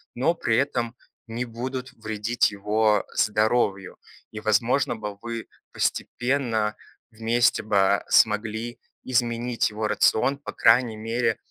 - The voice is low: Yes, low, 115 Hz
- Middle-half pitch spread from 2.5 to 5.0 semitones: No, narrow, 2.1 semitones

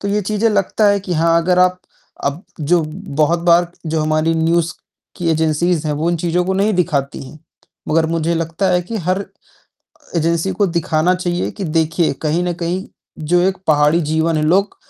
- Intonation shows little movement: Yes, narrow, 2.3 semitones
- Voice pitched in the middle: Yes, medium, 170 Hz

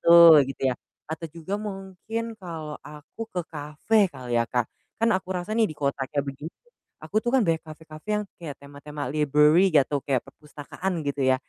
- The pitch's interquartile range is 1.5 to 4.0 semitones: No, average, 4.7 semitones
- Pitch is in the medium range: Yes, medium, 155 Hz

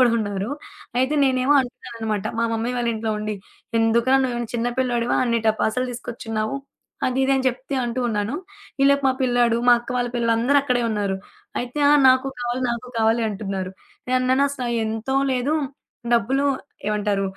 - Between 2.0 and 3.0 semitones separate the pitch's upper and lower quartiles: Yes, narrow, 2.5 semitones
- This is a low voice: No, high, 240 Hz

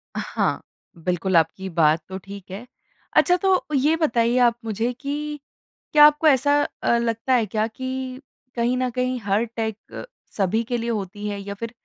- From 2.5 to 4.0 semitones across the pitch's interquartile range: No, average, 4.5 semitones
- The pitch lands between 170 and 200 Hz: No, high, 235 Hz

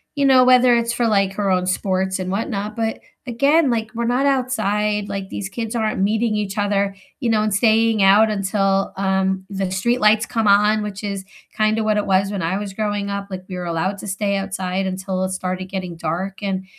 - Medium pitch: No, high, 200 Hz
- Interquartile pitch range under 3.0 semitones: Yes, narrow, 2.4 semitones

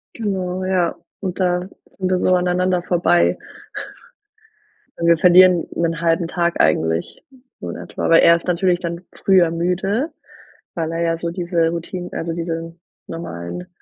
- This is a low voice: No, medium, 175 Hz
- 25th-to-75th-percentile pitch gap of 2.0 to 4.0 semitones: No, narrow, 1.5 semitones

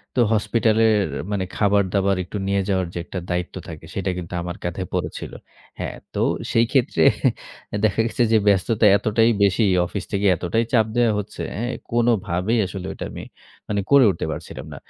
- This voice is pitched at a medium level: No, low, 100 Hz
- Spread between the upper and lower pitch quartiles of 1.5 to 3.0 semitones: No, average, 3.4 semitones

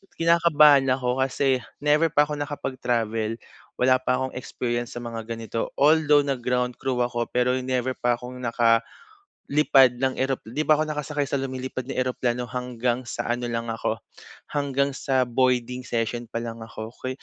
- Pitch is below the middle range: Yes, low, 125 Hz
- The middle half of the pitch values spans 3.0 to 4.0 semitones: No, narrow, 2.5 semitones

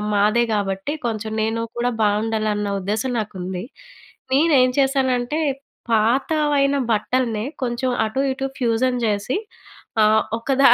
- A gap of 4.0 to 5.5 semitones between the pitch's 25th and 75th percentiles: No, average, 3.6 semitones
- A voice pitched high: Yes, high, 230 Hz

